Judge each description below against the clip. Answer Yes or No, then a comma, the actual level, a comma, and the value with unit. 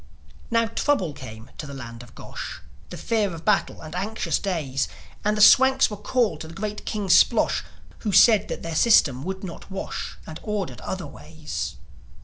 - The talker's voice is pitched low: No, high, 190 Hz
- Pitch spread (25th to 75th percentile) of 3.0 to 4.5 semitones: No, wide, 5.5 semitones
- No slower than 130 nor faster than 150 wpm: No, average, 180 wpm